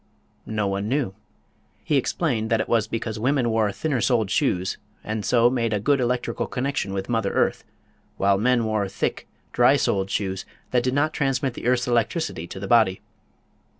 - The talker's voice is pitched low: Yes, low, 115 Hz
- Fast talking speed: No, average, 180 wpm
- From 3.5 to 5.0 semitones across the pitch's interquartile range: Yes, average, 3.9 semitones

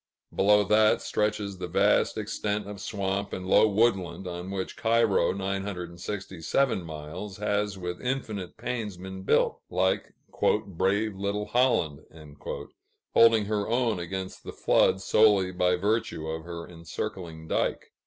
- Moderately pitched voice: No, very low, 95 Hz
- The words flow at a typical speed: No, slow, 130 wpm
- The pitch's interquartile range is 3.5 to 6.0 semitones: No, average, 2.8 semitones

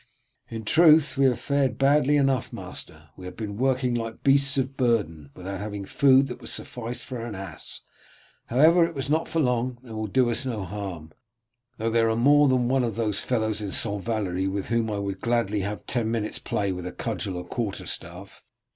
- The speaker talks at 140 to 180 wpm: No, average, 200 wpm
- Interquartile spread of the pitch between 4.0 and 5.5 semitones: Yes, average, 4.6 semitones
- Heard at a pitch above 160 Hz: No, low, 115 Hz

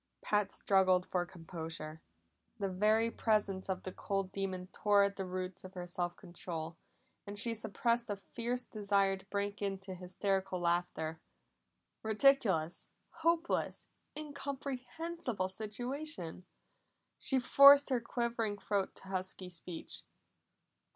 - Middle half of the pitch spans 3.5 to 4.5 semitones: Yes, average, 4.1 semitones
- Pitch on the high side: Yes, high, 195 Hz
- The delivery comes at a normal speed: No, slow, 120 wpm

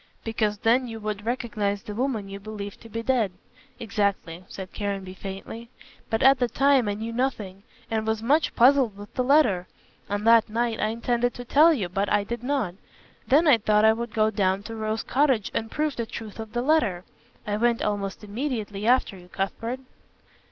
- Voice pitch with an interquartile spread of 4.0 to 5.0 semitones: No, average, 3.1 semitones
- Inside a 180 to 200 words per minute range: Yes, average, 195 wpm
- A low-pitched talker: No, high, 220 Hz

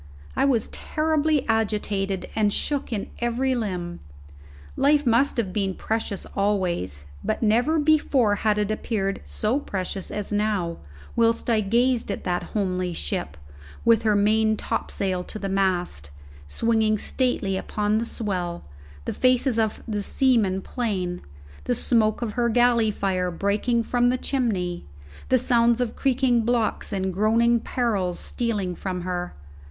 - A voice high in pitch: Yes, high, 215 Hz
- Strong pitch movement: No, average, 3.7 semitones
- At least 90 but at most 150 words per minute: Yes, average, 145 wpm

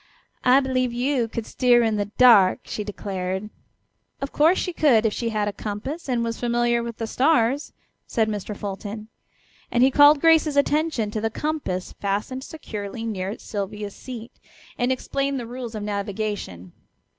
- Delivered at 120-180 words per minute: Yes, average, 165 wpm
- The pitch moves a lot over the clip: No, average, 3.9 semitones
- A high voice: Yes, high, 230 Hz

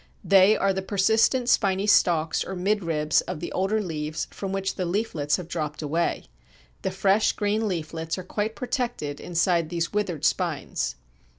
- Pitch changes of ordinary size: Yes, average, 4.0 semitones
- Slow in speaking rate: No, average, 160 wpm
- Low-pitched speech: No, medium, 185 Hz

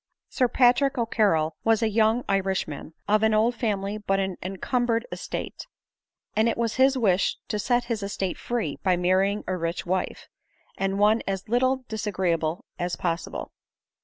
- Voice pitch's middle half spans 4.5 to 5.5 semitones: No, average, 3.8 semitones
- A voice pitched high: Yes, high, 210 Hz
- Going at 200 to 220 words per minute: No, average, 160 wpm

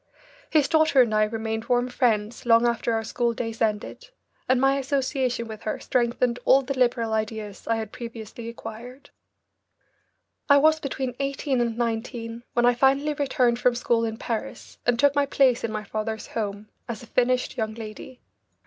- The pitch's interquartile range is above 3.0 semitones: No, average, 2.7 semitones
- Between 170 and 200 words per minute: Yes, average, 175 wpm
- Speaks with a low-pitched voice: No, high, 235 Hz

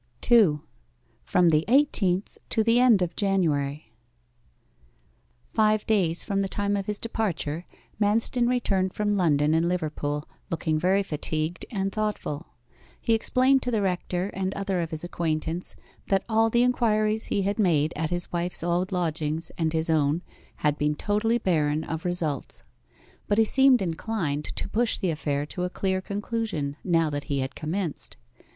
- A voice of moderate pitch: Yes, medium, 180 Hz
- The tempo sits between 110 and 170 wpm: Yes, average, 160 wpm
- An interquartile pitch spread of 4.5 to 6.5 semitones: Yes, average, 5.0 semitones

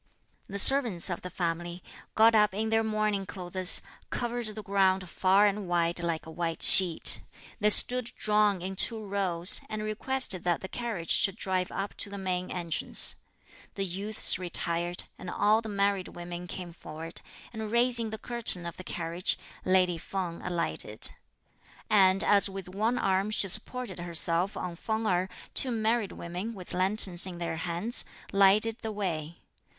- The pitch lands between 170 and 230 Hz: Yes, high, 190 Hz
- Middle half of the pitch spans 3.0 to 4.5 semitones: Yes, average, 3.4 semitones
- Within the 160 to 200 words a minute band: Yes, average, 165 wpm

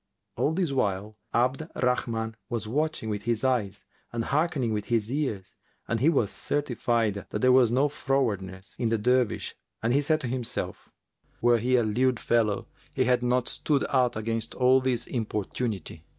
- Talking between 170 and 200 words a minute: Yes, average, 175 wpm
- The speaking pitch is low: Yes, low, 120 Hz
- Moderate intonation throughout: Yes, average, 3.0 semitones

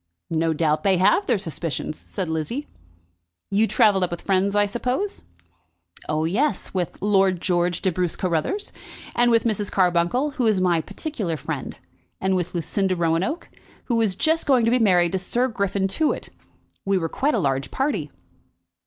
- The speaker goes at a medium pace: Yes, average, 170 wpm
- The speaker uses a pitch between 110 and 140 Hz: No, high, 190 Hz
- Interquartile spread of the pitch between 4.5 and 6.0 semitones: Yes, average, 5.0 semitones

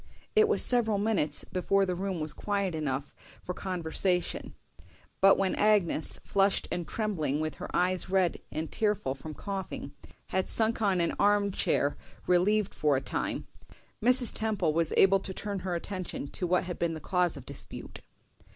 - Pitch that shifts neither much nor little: Yes, average, 3.6 semitones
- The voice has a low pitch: No, medium, 185 Hz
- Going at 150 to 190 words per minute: Yes, average, 170 wpm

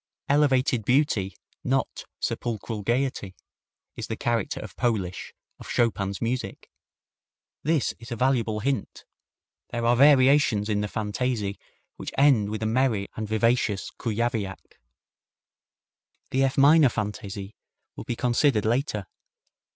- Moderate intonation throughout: Yes, average, 3.8 semitones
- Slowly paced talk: Yes, slow, 120 wpm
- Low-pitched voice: Yes, low, 115 Hz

